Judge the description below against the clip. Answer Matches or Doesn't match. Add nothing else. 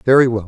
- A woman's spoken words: Doesn't match